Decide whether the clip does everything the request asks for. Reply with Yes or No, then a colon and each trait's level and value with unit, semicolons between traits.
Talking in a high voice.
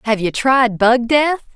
Yes: high, 245 Hz